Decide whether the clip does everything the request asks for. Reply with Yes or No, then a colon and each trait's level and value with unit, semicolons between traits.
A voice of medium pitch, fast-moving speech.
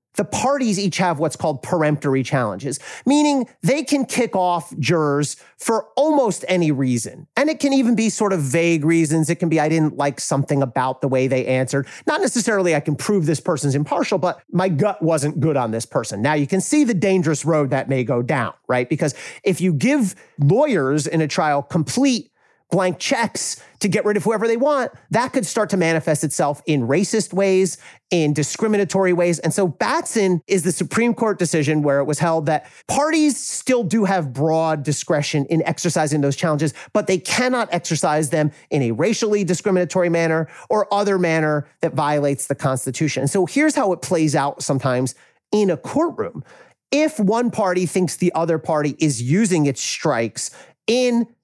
No: medium, 170 Hz; average, 185 wpm